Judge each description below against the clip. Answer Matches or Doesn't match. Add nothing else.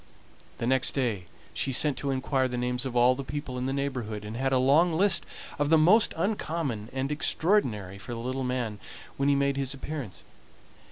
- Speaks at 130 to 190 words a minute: Doesn't match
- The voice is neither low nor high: Doesn't match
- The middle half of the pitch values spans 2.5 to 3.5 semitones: Matches